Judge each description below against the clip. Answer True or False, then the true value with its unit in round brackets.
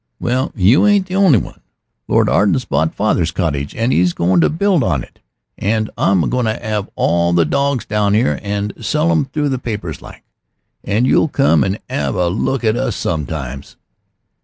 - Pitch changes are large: True (7.1 semitones)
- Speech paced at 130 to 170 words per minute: False (185 wpm)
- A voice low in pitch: True (105 Hz)